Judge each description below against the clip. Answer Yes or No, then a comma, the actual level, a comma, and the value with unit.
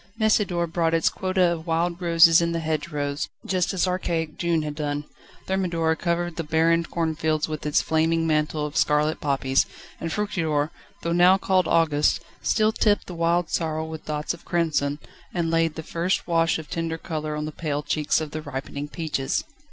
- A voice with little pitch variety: Yes, narrow, 2.0 semitones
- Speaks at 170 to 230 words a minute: Yes, average, 180 wpm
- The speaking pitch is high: No, medium, 165 Hz